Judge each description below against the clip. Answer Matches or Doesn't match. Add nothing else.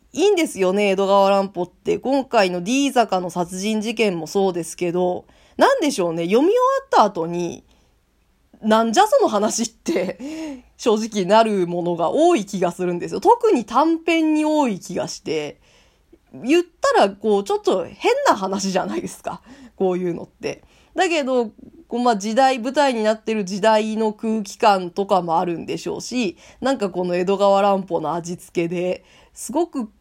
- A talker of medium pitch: Doesn't match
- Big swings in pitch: Matches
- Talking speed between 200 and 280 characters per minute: Doesn't match